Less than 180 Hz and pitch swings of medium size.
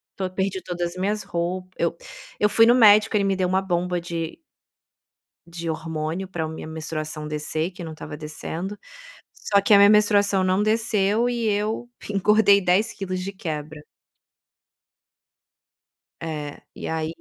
No: medium, 185 Hz; average, 3.9 semitones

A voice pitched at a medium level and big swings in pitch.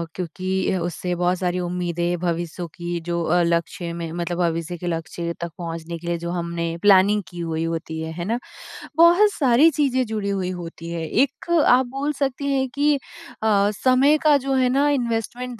Yes: medium, 180 Hz; wide, 6.8 semitones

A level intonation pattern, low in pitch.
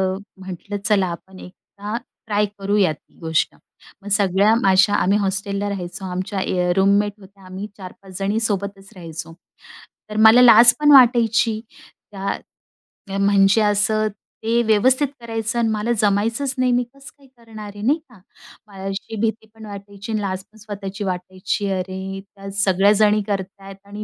No: narrow, 2.3 semitones; high, 205 Hz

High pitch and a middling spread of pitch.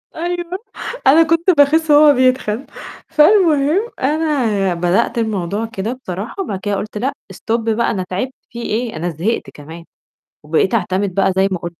No: high, 225 Hz; wide, 7.6 semitones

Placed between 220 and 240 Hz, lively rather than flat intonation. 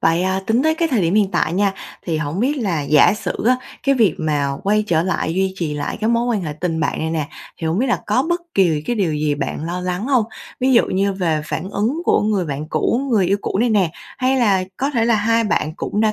No: high, 195 Hz; wide, 6.2 semitones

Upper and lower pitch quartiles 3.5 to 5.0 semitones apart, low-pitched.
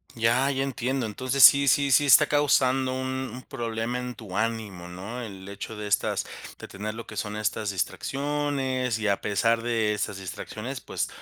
Yes: average, 3.8 semitones; low, 115 Hz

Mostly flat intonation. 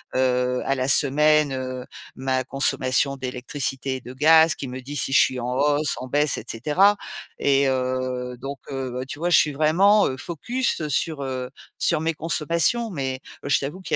No: average, 3.0 semitones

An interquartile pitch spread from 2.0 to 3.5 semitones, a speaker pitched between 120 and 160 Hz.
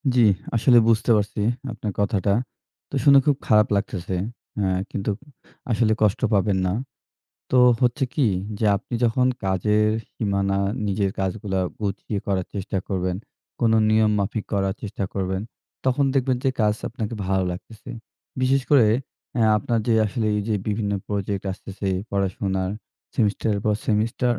No: average, 2.8 semitones; low, 105 Hz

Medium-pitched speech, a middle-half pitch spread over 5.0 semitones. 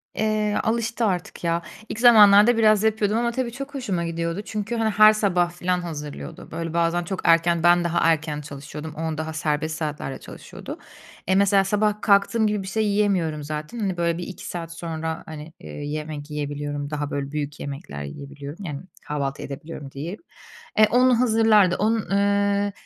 Yes: medium, 175 Hz; wide, 5.6 semitones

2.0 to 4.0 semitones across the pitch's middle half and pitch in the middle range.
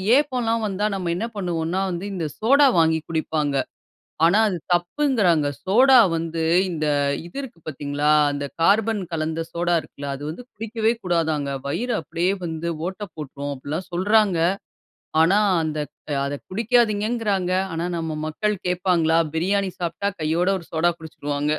No: average, 4.5 semitones; medium, 175 Hz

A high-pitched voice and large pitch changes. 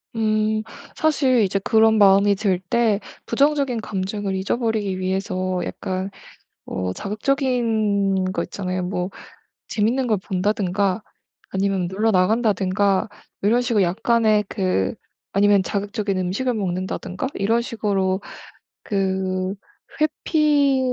No: high, 205 Hz; average, 3.1 semitones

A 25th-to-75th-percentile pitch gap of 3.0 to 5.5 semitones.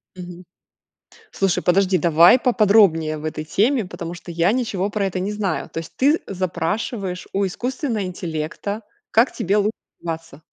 Yes: average, 3.9 semitones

